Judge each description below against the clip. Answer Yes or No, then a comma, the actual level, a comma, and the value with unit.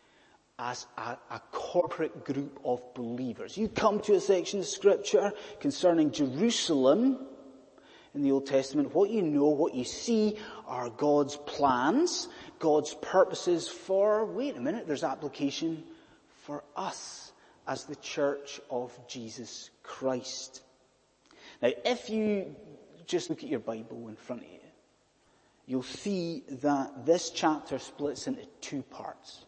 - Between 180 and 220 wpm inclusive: No, slow, 135 wpm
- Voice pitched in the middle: Yes, medium, 150 Hz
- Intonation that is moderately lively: No, wide, 7.8 semitones